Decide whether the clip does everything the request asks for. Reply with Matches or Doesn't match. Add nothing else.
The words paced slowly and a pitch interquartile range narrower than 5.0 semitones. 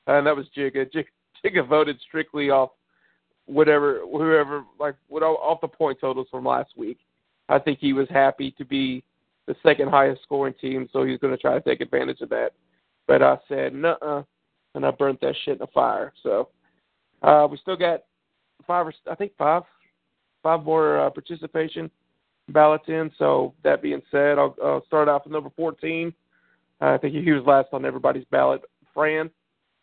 Doesn't match